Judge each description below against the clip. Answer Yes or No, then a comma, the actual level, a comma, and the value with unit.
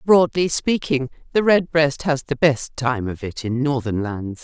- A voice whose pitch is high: No, medium, 140 Hz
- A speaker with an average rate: Yes, average, 175 wpm